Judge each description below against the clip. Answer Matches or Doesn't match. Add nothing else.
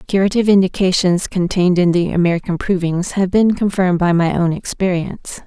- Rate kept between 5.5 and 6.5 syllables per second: Matches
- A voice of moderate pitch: Matches